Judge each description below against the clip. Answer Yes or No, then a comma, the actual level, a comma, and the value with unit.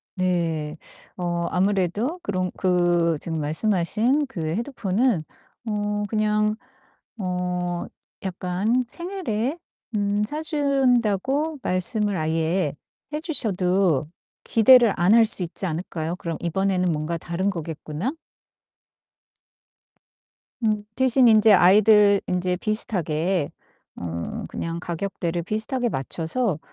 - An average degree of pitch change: Yes, average, 4.4 semitones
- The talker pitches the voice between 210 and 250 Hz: No, high, 190 Hz